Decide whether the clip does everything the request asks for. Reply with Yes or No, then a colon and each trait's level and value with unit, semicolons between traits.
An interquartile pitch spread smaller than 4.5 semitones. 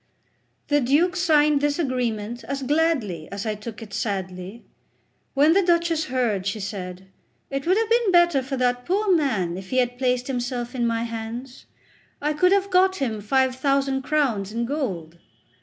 No: wide, 5.6 semitones